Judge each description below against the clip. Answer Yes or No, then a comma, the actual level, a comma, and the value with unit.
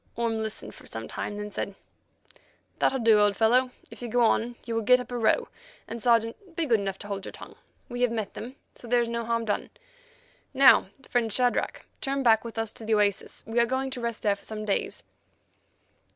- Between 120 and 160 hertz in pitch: No, high, 230 Hz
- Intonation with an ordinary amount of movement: No, narrow, 2.1 semitones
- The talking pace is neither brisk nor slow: No, fast, 220 wpm